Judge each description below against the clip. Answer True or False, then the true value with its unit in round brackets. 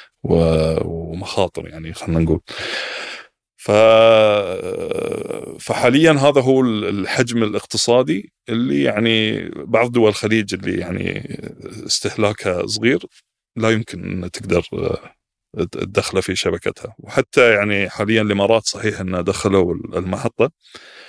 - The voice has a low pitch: True (110 Hz)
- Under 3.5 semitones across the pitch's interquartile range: False (4.5 semitones)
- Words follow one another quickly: False (95 wpm)